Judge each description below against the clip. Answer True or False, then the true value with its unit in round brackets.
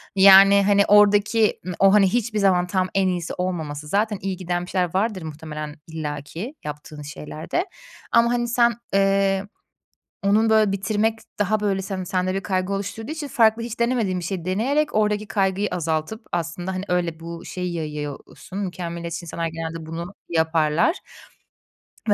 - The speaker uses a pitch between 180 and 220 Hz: True (190 Hz)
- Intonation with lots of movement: False (3.7 semitones)